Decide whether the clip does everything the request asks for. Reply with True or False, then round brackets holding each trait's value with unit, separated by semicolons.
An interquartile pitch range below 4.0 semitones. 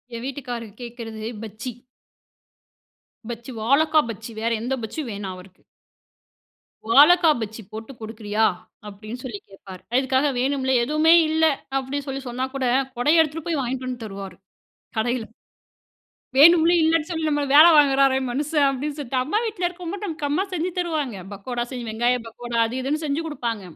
False (4.9 semitones)